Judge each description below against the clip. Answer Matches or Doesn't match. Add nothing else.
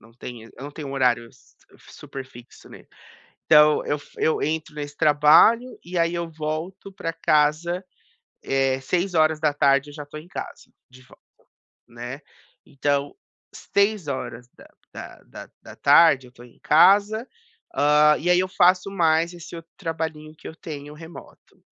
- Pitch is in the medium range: Matches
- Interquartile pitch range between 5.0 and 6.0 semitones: Doesn't match